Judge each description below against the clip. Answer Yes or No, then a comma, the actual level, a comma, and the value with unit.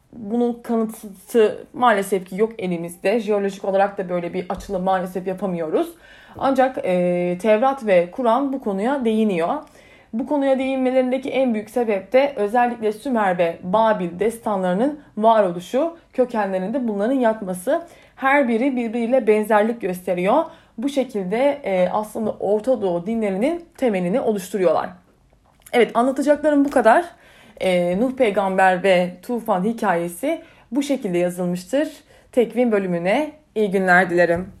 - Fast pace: No, average, 120 wpm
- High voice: Yes, high, 220 Hz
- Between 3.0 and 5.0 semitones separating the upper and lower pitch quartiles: No, wide, 5.5 semitones